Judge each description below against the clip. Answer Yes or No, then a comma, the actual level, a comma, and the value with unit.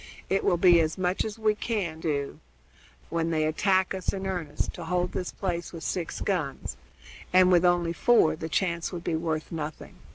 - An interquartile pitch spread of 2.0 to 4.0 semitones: Yes, narrow, 2.6 semitones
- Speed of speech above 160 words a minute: Yes, average, 190 wpm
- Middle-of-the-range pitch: Yes, medium, 175 Hz